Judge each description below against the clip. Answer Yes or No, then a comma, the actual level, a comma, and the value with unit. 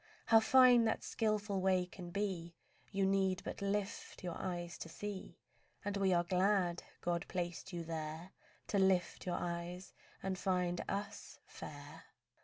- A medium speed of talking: Yes, average, 150 wpm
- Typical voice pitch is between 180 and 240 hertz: Yes, medium, 185 Hz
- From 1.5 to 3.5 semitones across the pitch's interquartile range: Yes, narrow, 2.5 semitones